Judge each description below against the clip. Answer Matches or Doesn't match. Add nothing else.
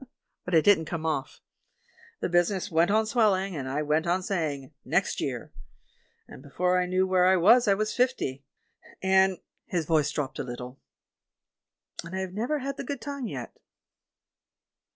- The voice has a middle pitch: Matches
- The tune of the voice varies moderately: Matches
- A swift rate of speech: Doesn't match